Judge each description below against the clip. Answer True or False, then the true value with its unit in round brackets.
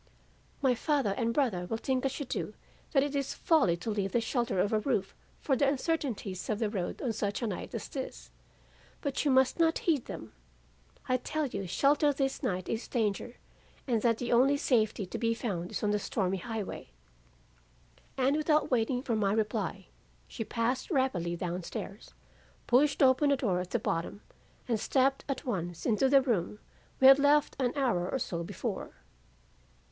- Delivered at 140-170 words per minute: False (185 wpm)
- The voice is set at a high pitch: True (235 Hz)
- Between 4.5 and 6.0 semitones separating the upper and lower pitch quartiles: True (5.2 semitones)